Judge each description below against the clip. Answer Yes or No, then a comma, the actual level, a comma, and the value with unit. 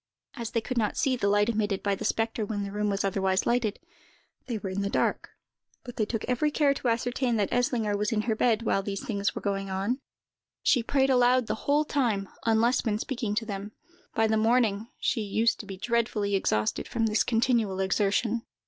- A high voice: Yes, high, 220 Hz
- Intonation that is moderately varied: Yes, average, 3.1 semitones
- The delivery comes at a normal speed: No, fast, 210 wpm